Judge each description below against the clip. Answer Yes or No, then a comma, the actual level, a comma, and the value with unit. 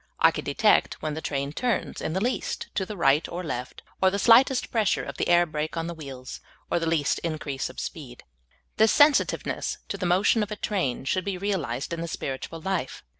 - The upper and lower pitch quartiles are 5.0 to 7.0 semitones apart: Yes, wide, 5.4 semitones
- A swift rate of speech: Yes, fast, 215 wpm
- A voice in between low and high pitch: Yes, medium, 170 Hz